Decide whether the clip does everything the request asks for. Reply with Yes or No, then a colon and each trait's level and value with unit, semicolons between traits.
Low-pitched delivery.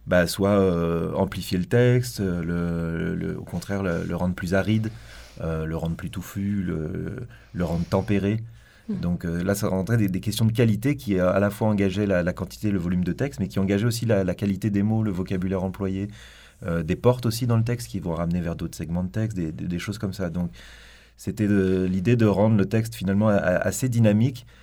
Yes: very low, 95 Hz